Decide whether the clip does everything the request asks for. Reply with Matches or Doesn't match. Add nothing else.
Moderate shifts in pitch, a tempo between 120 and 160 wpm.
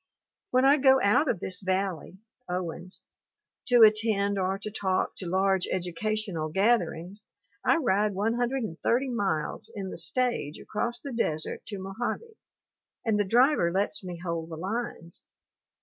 Matches